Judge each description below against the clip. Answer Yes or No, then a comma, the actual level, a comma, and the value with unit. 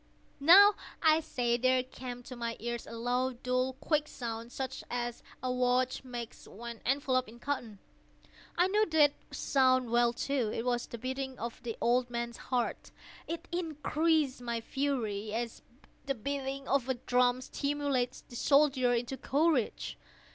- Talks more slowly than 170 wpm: Yes, average, 155 wpm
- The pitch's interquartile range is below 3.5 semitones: Yes, average, 2.7 semitones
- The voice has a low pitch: No, very high, 255 Hz